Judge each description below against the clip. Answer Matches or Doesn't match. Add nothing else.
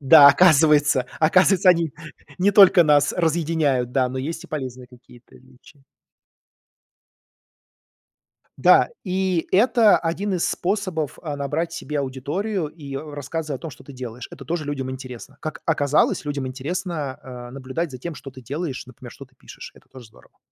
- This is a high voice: Doesn't match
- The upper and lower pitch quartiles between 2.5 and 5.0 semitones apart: Matches